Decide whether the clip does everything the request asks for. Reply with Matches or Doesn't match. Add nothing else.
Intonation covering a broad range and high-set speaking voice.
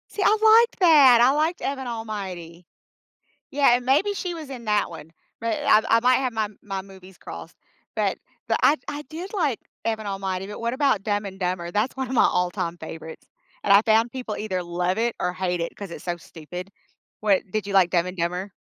Matches